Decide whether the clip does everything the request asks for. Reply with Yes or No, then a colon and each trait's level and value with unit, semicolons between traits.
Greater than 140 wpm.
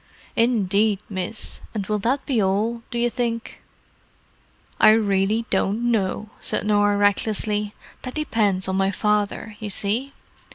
No: slow, 135 wpm